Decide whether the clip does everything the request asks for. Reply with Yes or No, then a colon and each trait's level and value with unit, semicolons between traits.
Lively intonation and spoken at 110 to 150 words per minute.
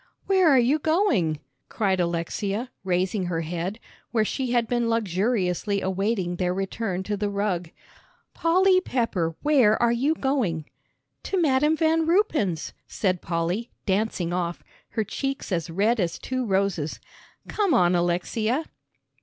Yes: wide, 6.3 semitones; slow, 135 wpm